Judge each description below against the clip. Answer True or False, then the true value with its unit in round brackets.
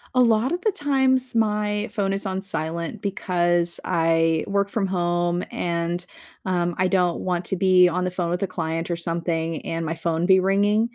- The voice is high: False (180 Hz)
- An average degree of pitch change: True (3.0 semitones)